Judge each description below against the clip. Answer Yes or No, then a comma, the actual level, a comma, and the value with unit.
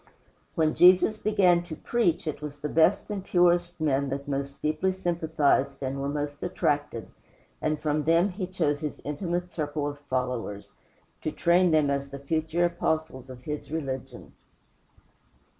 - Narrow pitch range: No, average, 3.6 semitones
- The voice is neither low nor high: Yes, medium, 155 Hz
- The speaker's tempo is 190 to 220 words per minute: No, average, 155 wpm